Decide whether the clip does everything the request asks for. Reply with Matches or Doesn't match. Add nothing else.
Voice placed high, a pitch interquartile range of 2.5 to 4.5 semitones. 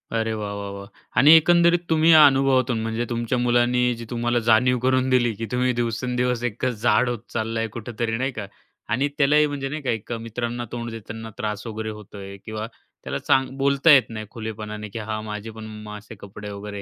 Doesn't match